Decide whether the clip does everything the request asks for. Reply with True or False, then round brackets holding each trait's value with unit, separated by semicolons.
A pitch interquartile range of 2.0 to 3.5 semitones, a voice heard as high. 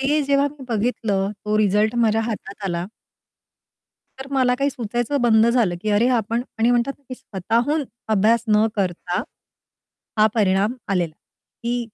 True (3.1 semitones; 225 Hz)